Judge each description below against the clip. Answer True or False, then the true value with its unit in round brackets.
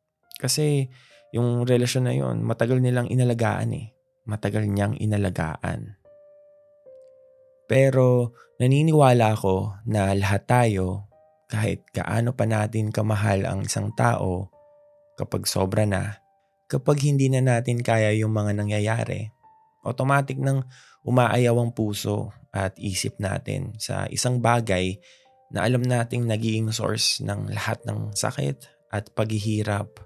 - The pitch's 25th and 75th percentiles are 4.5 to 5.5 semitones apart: False (4.0 semitones)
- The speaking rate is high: False (120 wpm)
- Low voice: True (120 Hz)